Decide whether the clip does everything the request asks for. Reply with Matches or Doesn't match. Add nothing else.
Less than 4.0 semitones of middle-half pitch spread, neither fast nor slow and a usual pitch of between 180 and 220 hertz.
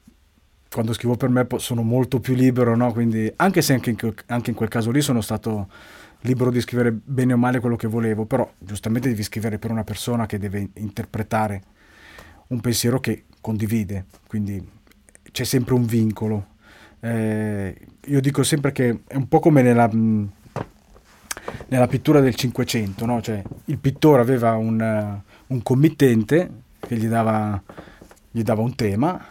Doesn't match